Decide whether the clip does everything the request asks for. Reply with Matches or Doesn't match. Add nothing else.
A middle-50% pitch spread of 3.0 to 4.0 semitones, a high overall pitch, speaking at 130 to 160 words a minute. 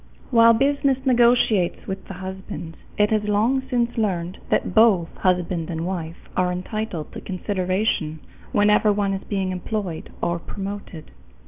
Matches